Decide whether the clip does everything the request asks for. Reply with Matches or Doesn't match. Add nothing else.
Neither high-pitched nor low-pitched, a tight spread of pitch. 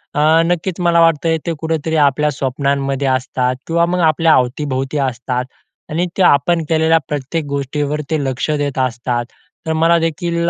Doesn't match